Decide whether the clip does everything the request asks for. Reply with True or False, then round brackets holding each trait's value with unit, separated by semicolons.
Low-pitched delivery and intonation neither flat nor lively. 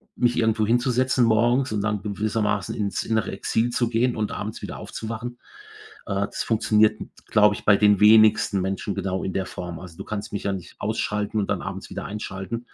False (105 Hz; 2.1 semitones)